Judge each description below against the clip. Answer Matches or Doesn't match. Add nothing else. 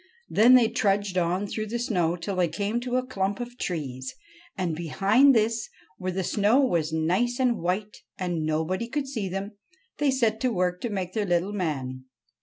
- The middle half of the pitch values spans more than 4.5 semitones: Matches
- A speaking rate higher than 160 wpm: Matches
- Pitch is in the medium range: Doesn't match